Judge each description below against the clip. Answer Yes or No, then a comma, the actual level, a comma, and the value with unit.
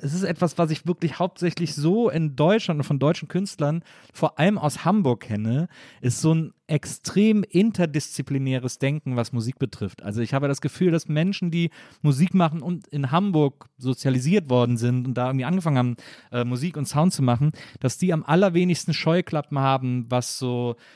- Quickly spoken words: No, average, 180 wpm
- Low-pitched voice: No, medium, 150 Hz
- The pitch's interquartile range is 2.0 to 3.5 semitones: No, average, 5.2 semitones